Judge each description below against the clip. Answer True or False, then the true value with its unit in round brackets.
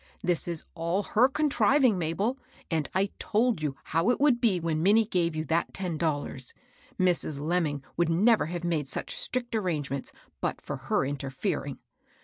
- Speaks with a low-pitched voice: False (175 Hz)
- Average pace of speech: True (165 wpm)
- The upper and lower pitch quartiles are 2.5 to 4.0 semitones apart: False (5.5 semitones)